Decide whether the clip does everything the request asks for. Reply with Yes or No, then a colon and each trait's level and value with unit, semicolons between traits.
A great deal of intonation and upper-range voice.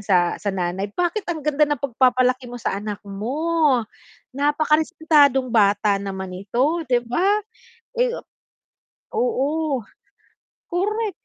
Yes: wide, 7.3 semitones; very high, 265 Hz